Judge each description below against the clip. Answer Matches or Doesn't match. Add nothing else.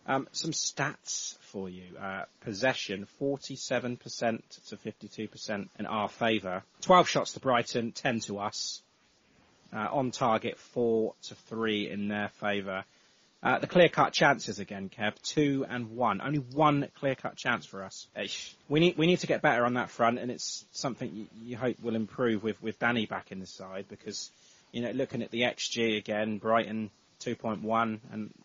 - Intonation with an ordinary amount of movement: Matches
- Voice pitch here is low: Matches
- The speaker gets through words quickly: Doesn't match